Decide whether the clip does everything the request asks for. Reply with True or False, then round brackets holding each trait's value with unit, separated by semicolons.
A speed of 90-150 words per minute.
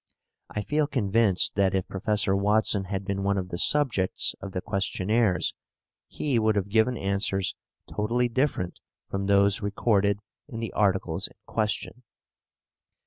True (140 wpm)